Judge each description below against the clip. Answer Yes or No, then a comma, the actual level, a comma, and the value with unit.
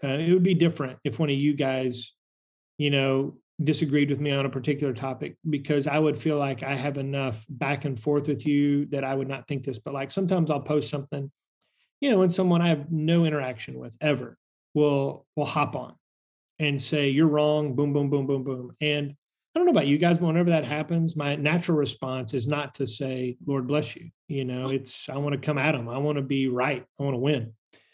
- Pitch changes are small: Yes, narrow, 2.0 semitones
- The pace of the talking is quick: Yes, fast, 230 wpm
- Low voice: No, medium, 145 Hz